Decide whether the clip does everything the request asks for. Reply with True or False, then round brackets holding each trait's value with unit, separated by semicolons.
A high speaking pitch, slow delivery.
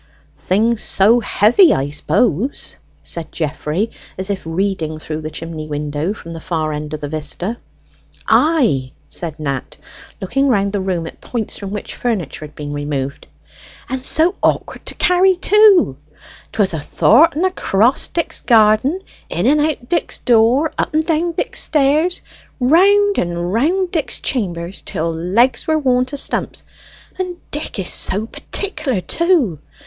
False (215 Hz; 150 wpm)